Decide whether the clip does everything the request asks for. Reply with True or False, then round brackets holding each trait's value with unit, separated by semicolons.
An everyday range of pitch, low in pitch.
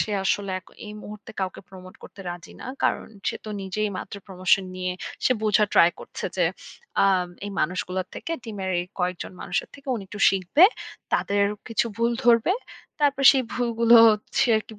False (3.8 semitones; 205 Hz)